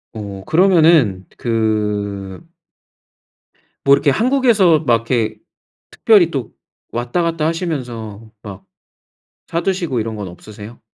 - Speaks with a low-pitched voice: Yes, low, 120 Hz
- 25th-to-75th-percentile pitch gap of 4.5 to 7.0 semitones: No, wide, 7.7 semitones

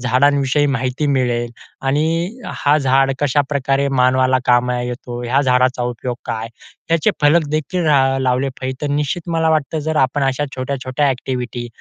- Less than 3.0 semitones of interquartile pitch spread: Yes, narrow, 2.5 semitones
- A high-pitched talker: No, low, 135 Hz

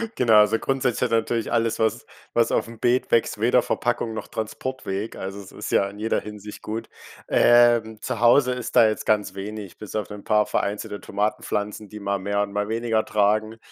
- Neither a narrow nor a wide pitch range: No, narrow, 2.1 semitones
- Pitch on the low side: Yes, low, 110 Hz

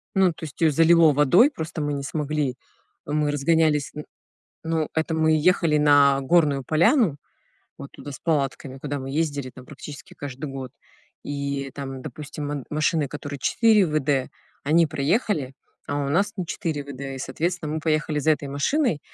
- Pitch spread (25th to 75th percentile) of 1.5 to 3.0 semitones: Yes, narrow, 2.6 semitones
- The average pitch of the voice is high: No, medium, 150 Hz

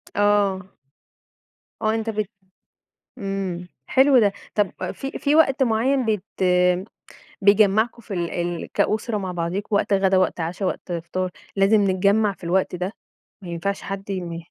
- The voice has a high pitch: Yes, high, 195 Hz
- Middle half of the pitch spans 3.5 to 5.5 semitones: No, average, 2.9 semitones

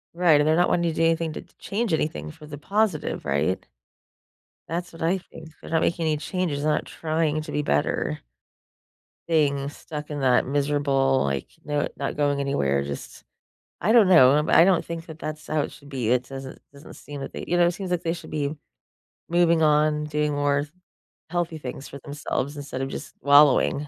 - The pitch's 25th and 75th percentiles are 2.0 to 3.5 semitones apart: Yes, average, 2.7 semitones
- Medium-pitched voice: Yes, medium, 150 Hz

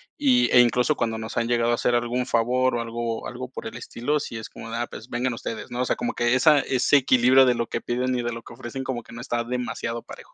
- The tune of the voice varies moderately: No, narrow, 1.5 semitones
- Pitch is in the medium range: No, low, 120 Hz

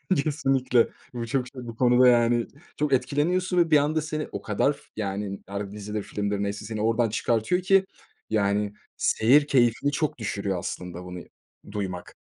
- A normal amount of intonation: No, wide, 5.7 semitones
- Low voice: Yes, low, 115 Hz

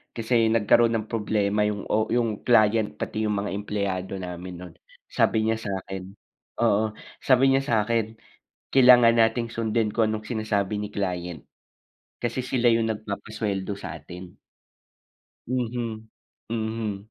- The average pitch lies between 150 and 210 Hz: No, low, 110 Hz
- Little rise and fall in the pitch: Yes, narrow, 2.2 semitones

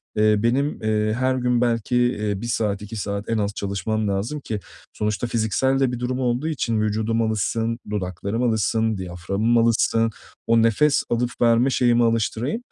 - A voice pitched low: Yes, low, 115 Hz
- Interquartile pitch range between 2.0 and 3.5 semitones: Yes, narrow, 2.4 semitones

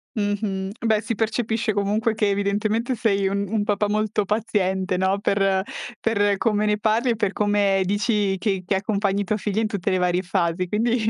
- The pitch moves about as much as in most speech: No, narrow, 1.9 semitones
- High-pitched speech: Yes, high, 205 Hz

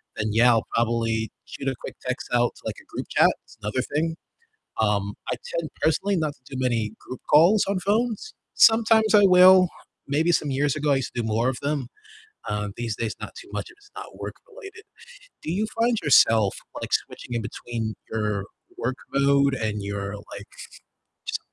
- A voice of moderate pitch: No, low, 130 Hz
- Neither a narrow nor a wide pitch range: No, wide, 7.3 semitones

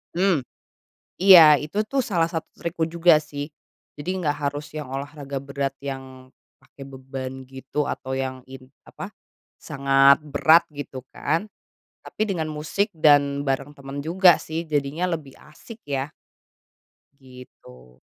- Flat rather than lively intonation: No, average, 3.1 semitones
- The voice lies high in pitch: No, medium, 145 Hz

